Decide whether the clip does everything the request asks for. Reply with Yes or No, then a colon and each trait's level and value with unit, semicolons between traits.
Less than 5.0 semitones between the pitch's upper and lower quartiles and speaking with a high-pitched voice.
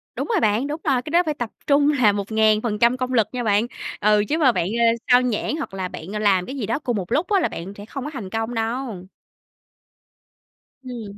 Yes: average, 4.3 semitones; high, 235 Hz